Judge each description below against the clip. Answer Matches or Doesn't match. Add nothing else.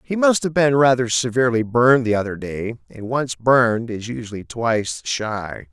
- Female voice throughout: Doesn't match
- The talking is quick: Doesn't match